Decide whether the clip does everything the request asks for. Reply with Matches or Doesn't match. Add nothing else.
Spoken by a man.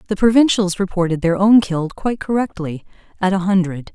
Doesn't match